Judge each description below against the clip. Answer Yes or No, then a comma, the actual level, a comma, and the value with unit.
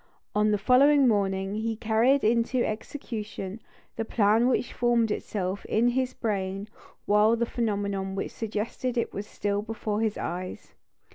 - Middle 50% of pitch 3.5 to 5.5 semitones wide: No, narrow, 2.6 semitones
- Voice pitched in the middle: No, high, 215 Hz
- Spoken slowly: No, average, 145 wpm